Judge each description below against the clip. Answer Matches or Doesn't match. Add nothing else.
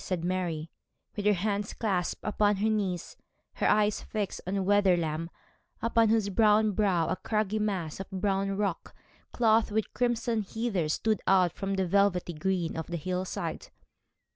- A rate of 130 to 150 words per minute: Doesn't match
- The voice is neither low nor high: Doesn't match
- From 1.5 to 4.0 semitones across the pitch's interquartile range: Matches